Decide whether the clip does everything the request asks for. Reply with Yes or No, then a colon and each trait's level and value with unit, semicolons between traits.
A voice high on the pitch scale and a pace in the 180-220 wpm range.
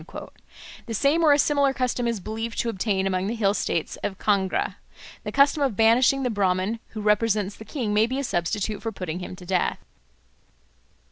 Yes: high, 220 Hz; average, 190 wpm